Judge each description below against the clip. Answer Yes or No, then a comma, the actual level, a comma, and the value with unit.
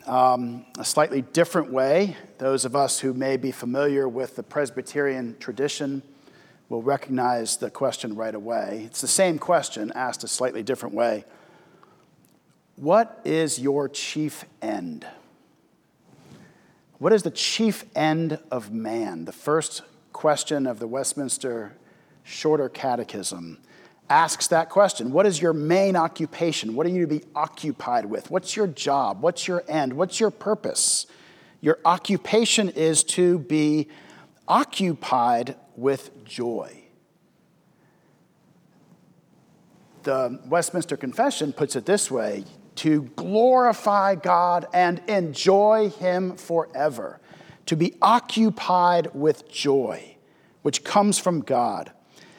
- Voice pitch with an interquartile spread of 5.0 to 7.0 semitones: Yes, average, 5.3 semitones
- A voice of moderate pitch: Yes, medium, 155 Hz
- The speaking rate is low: Yes, slow, 120 wpm